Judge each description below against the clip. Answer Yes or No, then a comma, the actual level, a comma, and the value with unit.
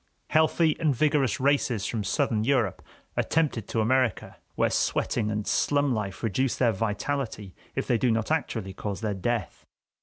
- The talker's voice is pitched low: Yes, low, 115 Hz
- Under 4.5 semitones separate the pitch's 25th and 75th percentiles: No, average, 4.8 semitones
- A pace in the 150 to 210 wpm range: Yes, average, 160 wpm